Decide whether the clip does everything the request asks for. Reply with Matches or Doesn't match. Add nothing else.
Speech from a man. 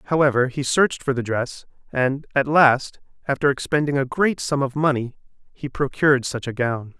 Matches